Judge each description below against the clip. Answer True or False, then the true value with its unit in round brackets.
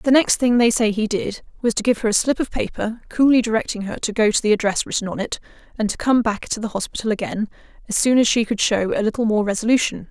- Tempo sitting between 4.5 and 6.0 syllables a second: False (6.3 syllables/s)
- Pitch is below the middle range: False (220 Hz)